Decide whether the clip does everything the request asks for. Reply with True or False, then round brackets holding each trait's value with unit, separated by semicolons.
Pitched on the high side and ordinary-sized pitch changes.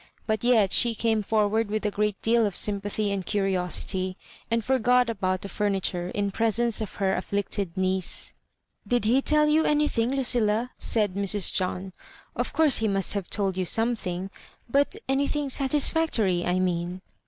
True (210 Hz; 3.9 semitones)